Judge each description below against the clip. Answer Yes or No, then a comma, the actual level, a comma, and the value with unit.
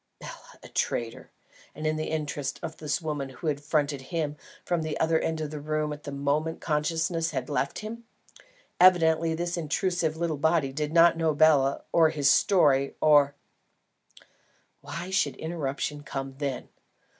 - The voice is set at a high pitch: No, medium, 155 Hz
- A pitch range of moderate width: No, narrow, 2.3 semitones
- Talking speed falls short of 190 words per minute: Yes, average, 160 wpm